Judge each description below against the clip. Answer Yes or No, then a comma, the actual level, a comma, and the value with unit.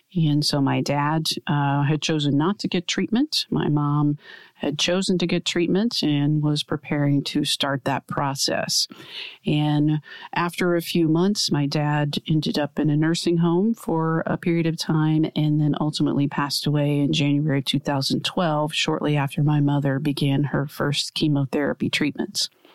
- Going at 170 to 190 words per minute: No, average, 160 wpm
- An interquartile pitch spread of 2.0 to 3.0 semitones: Yes, average, 2.7 semitones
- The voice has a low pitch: No, medium, 150 Hz